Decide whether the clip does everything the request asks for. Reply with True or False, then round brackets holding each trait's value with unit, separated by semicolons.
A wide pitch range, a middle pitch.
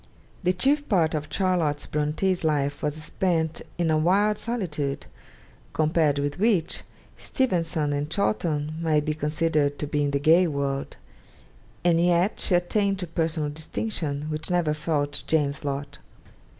False (3.3 semitones; 155 Hz)